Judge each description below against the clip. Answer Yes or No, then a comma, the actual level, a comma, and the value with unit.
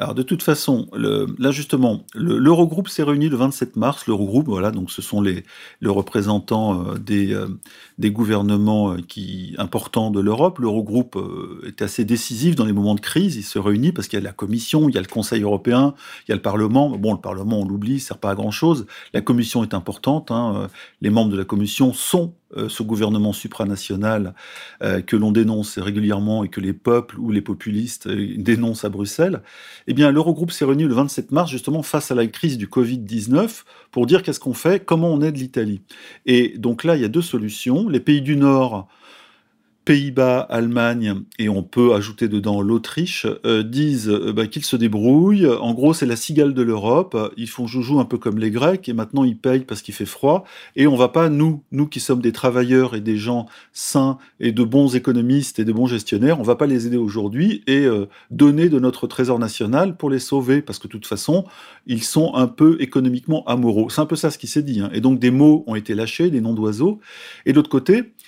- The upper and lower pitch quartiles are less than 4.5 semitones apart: No, average, 4.8 semitones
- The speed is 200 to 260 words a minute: Yes, average, 215 wpm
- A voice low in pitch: Yes, low, 120 Hz